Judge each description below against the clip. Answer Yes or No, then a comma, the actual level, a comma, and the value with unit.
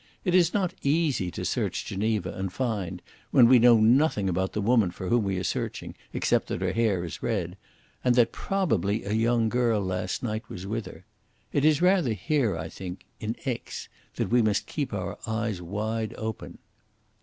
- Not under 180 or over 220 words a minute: Yes, average, 190 wpm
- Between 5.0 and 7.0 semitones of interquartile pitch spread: No, average, 4.4 semitones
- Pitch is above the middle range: No, low, 110 Hz